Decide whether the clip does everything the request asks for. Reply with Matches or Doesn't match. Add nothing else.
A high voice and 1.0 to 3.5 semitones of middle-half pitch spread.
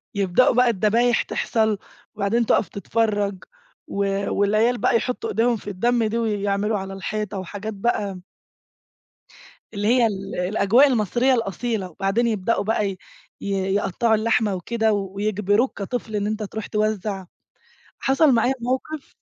Matches